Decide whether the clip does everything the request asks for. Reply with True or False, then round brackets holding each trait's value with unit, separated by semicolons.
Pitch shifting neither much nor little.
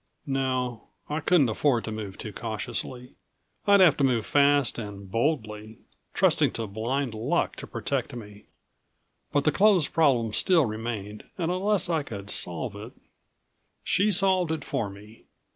False (6.2 semitones)